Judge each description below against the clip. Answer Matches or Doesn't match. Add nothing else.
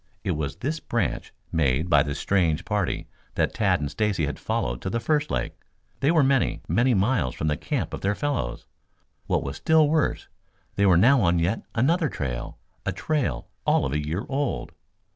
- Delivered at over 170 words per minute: Matches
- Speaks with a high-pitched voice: Doesn't match